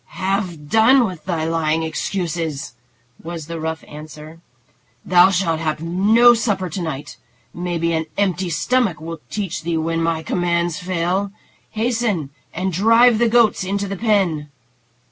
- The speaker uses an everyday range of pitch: Yes, average, 3.8 semitones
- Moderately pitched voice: Yes, medium, 175 Hz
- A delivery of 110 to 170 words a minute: Yes, average, 145 wpm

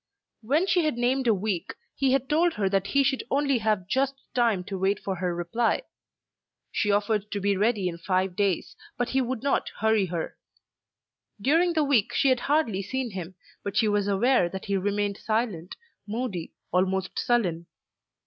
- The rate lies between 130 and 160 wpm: No, average, 180 wpm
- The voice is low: No, high, 210 Hz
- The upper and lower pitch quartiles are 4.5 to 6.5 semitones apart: Yes, average, 5.3 semitones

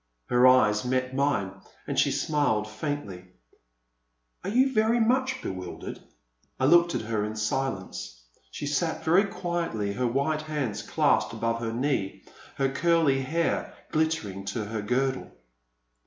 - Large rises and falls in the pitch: Yes, wide, 6.8 semitones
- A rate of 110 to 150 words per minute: Yes, average, 140 wpm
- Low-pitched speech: Yes, low, 130 Hz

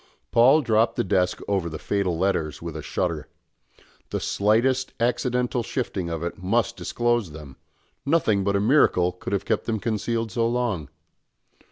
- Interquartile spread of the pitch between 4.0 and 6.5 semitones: Yes, average, 4.8 semitones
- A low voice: Yes, low, 105 Hz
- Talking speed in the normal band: Yes, average, 160 wpm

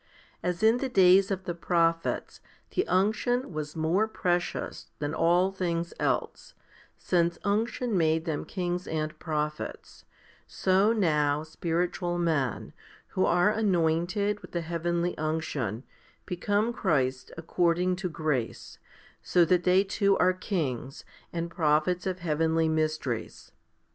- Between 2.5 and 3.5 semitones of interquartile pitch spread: Yes, average, 2.9 semitones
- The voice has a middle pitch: Yes, medium, 175 Hz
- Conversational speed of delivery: No, slow, 125 wpm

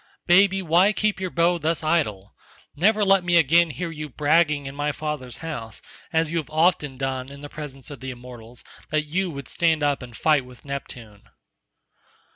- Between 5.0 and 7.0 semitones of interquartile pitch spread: No, average, 4.1 semitones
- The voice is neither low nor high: Yes, medium, 150 Hz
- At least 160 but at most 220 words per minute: Yes, average, 185 wpm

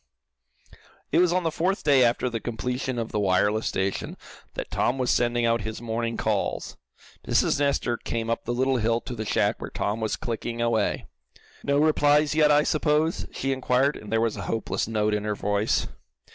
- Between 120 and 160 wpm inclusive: No, average, 190 wpm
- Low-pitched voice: Yes, low, 120 Hz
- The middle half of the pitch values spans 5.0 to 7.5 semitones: No, average, 4.1 semitones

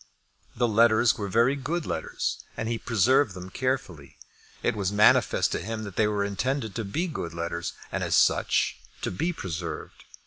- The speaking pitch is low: Yes, low, 110 Hz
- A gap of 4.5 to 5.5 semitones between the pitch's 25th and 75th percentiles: Yes, average, 5.2 semitones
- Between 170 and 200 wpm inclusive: Yes, average, 175 wpm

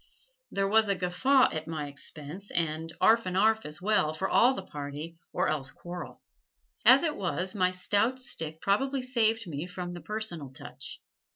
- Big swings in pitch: Yes, wide, 5.7 semitones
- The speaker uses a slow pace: No, average, 175 wpm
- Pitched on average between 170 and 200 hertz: Yes, medium, 185 Hz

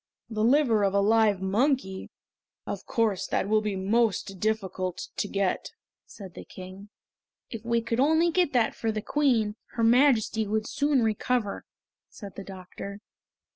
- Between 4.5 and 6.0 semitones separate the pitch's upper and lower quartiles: No, average, 3.1 semitones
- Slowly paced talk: No, average, 155 wpm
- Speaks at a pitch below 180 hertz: No, high, 220 Hz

